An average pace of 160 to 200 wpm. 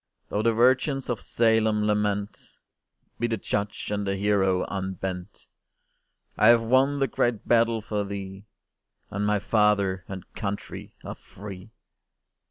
No: slow, 135 wpm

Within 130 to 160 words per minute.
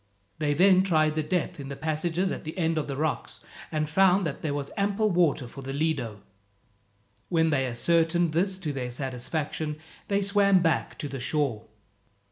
No: average, 180 wpm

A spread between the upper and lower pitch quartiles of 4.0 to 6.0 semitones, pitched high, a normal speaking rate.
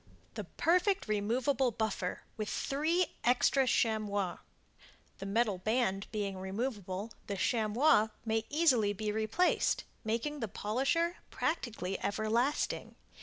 No: average, 4.6 semitones; high, 220 Hz; slow, 110 wpm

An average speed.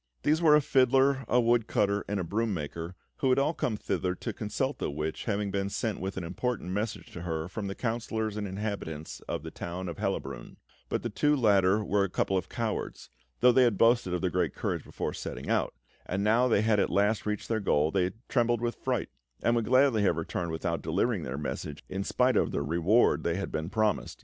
No: fast, 225 wpm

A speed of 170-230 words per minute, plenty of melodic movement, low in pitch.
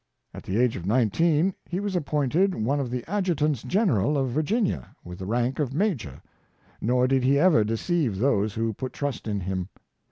Yes: average, 190 wpm; wide, 6.3 semitones; low, 130 Hz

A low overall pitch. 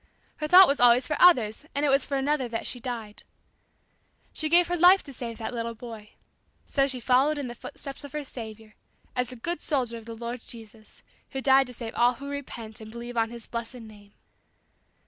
No: high, 245 Hz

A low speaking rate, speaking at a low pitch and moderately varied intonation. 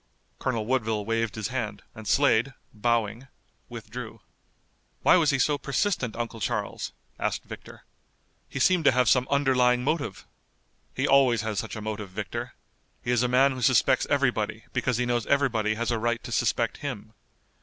No: average, 165 wpm; low, 120 Hz; average, 3.0 semitones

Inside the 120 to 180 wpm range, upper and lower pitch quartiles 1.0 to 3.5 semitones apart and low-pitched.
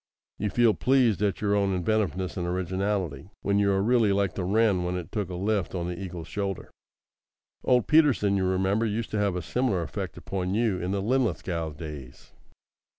No: average, 190 wpm; average, 3.0 semitones; low, 100 Hz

